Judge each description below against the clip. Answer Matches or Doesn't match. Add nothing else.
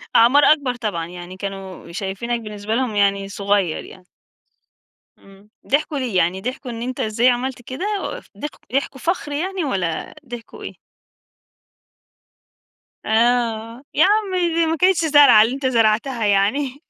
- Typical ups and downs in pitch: Doesn't match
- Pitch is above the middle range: Matches